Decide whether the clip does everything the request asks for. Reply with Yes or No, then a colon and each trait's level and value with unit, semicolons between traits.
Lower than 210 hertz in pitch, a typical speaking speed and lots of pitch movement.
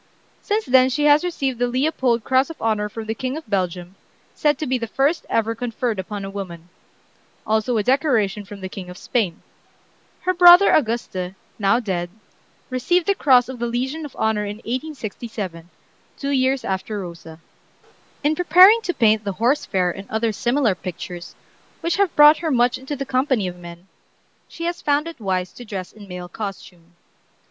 No: high, 235 Hz; average, 180 wpm; wide, 6.1 semitones